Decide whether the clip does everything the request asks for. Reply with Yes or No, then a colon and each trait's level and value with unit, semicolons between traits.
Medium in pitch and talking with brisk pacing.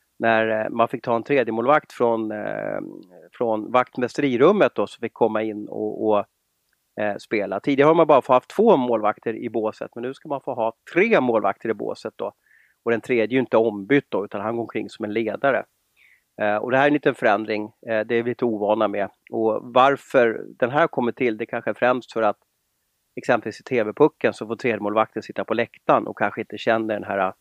No: low, 115 Hz; fast, 210 wpm